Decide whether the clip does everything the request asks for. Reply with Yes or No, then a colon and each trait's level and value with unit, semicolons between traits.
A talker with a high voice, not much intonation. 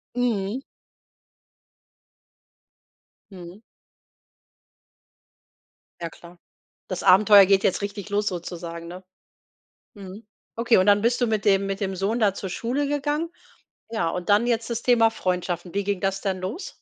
No: high, 200 Hz; average, 3.5 semitones